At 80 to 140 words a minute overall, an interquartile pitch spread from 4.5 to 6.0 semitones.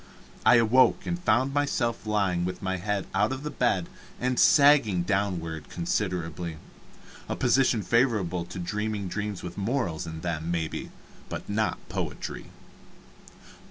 Yes: slow, 135 wpm; average, 5.0 semitones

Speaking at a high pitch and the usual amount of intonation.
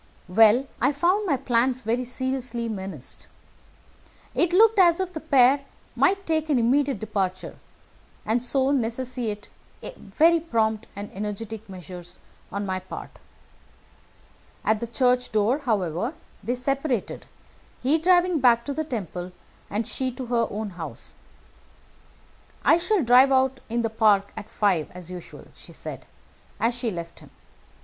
Yes: high, 240 Hz; average, 4.9 semitones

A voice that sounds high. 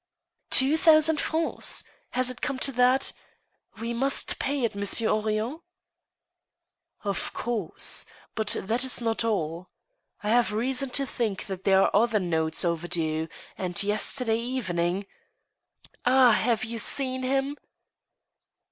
Yes: high, 230 Hz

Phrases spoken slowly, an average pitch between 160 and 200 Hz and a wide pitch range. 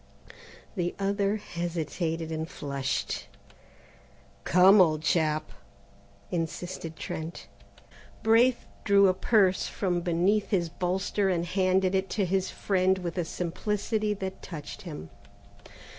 No: slow, 115 wpm; medium, 185 Hz; average, 2.9 semitones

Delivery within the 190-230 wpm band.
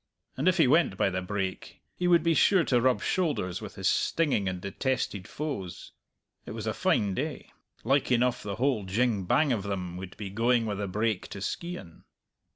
Yes: average, 195 wpm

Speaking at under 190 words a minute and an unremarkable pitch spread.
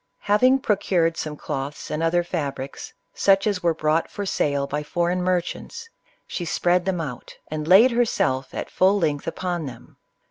Yes: average, 170 wpm; average, 4.2 semitones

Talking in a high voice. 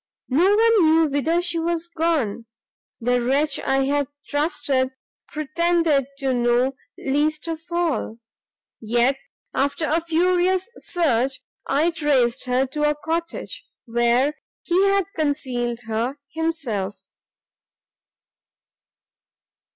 Yes: very high, 290 Hz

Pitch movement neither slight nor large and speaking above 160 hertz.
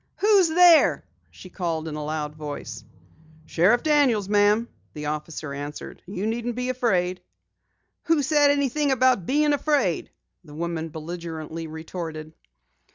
No: wide, 8.8 semitones; medium, 185 Hz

